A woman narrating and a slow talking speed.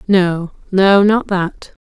Yes: female; slow, 130 wpm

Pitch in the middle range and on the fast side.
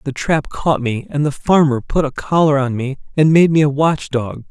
Yes: medium, 145 Hz; fast, 225 wpm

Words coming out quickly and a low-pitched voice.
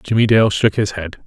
Yes: fast, 235 wpm; low, 105 Hz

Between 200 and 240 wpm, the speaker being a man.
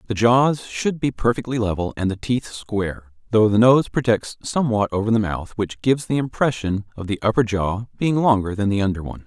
Yes: fast, 205 wpm; male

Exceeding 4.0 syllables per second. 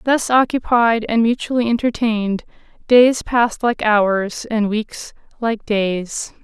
No: 3.8 syllables/s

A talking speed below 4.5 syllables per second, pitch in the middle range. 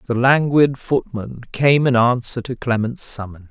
No: 4.3 syllables/s; low, 120 Hz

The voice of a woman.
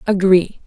Yes: female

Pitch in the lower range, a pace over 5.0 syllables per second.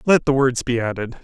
Yes: low, 130 Hz; 5.4 syllables/s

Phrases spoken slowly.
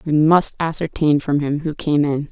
No: fast, 205 wpm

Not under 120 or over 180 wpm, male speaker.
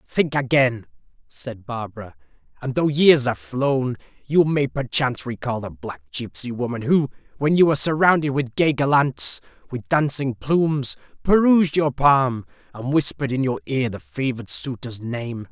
Yes: average, 155 wpm; male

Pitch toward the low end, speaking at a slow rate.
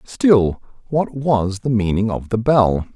No: low, 115 Hz; average, 165 wpm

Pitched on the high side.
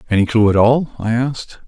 No: low, 115 Hz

